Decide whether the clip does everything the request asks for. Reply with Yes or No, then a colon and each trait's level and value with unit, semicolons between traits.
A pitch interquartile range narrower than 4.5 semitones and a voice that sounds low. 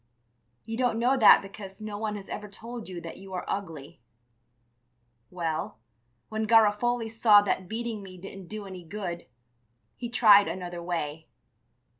No: average, 3.7 semitones; high, 205 Hz